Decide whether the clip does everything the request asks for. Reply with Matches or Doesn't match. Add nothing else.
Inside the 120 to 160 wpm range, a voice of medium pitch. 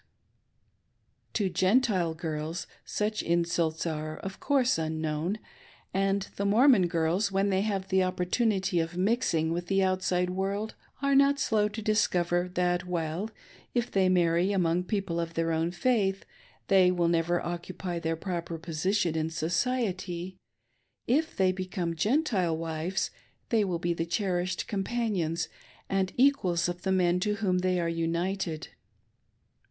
Matches